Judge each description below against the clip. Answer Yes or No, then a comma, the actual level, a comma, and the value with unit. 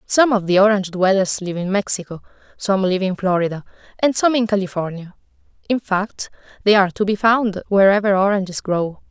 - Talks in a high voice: Yes, high, 195 Hz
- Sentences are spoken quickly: No, average, 170 wpm